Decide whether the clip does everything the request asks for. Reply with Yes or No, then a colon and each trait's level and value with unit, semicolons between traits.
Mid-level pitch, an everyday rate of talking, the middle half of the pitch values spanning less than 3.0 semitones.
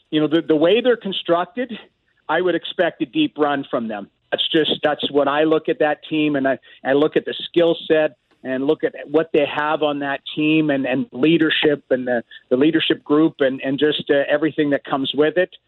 No: medium, 155 Hz; fast, 220 wpm; narrow, 2.5 semitones